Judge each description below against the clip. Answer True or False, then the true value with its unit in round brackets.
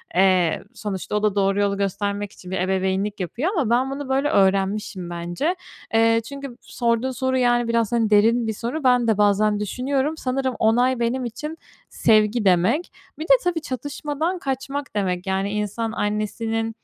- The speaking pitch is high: True (225 Hz)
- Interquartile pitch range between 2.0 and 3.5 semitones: False (4.4 semitones)